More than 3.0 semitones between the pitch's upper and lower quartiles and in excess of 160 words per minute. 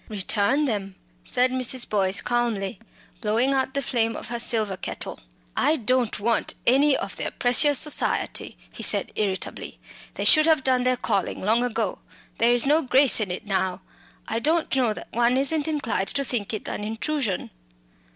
Yes: average, 4.1 semitones; average, 170 wpm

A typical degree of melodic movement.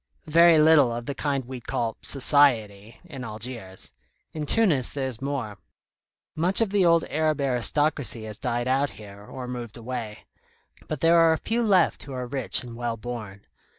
Yes: average, 4.8 semitones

